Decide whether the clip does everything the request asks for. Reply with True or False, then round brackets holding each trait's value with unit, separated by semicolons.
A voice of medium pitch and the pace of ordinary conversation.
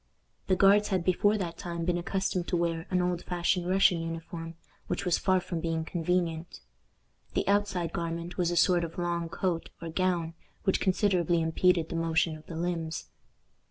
True (175 Hz; 175 wpm)